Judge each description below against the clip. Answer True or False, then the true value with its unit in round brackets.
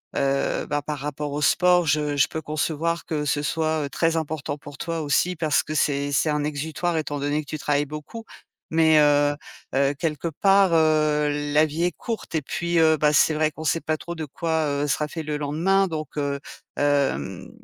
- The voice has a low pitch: False (150 Hz)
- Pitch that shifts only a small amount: True (1.9 semitones)